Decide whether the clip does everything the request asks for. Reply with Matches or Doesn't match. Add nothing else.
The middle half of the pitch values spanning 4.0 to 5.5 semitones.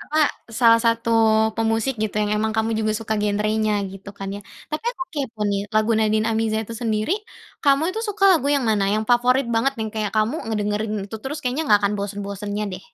Doesn't match